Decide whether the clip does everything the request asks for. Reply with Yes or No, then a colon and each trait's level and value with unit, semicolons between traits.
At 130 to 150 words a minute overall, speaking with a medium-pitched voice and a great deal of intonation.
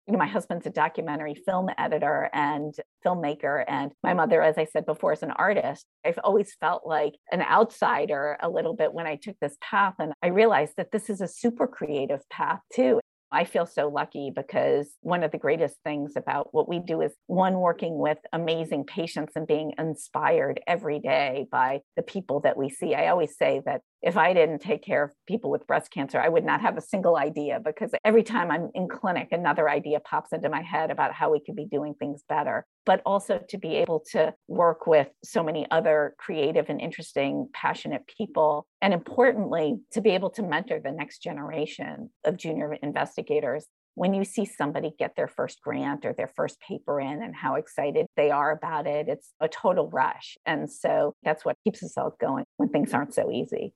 No: fast, 205 wpm; medium, 170 Hz; wide, 6.2 semitones